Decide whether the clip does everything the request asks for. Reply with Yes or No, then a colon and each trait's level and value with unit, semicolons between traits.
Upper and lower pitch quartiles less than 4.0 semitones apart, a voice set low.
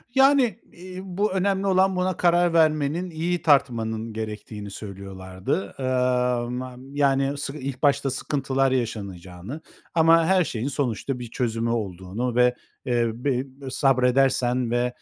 No: wide, 5.6 semitones; low, 130 Hz